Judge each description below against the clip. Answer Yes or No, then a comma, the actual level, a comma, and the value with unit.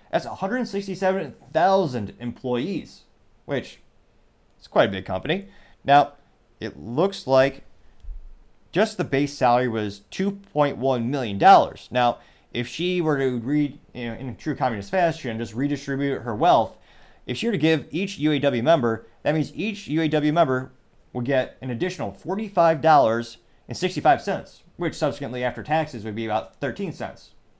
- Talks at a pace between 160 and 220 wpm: No, average, 140 wpm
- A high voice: No, low, 135 Hz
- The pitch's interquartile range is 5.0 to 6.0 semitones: Yes, wide, 5.6 semitones